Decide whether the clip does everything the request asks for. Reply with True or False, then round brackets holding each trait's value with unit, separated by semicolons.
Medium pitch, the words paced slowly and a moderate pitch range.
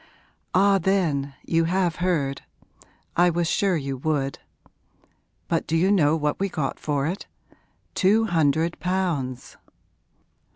True (165 Hz; 125 wpm; 4.2 semitones)